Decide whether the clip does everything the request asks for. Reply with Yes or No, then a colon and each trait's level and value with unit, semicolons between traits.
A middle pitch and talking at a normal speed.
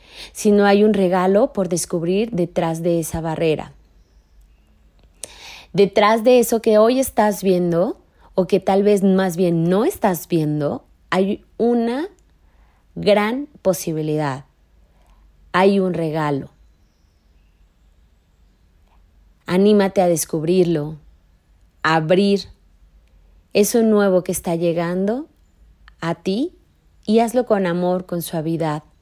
No: medium, 175 Hz; slow, 110 wpm